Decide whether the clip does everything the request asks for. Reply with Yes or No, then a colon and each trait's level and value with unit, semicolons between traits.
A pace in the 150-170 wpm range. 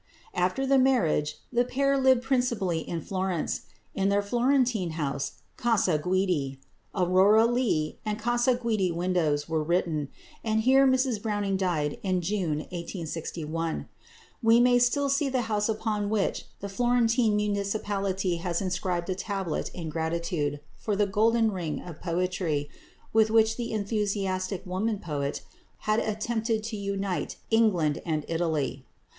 No: average, 140 wpm